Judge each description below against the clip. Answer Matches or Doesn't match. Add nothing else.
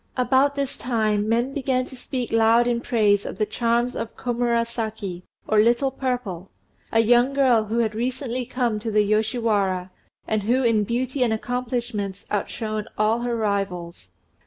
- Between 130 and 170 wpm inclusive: Matches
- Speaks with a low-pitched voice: Doesn't match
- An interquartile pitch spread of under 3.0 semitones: Matches